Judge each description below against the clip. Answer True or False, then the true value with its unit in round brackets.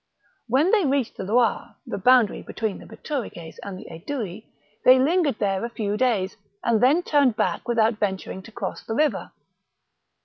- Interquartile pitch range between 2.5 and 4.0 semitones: False (4.4 semitones)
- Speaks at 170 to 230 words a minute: True (180 wpm)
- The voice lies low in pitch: False (230 Hz)